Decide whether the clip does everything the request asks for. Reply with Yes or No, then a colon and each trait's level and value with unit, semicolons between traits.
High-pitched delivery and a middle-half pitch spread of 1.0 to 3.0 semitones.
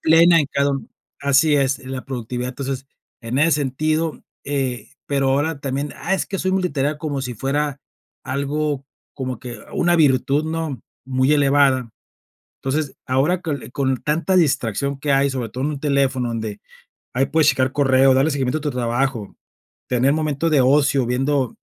No: medium, 140 Hz; narrow, 2.4 semitones